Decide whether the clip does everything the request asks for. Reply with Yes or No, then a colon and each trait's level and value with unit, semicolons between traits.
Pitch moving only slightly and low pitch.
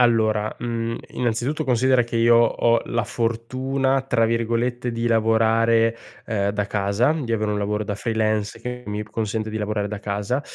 Yes: narrow, 1.9 semitones; low, 115 Hz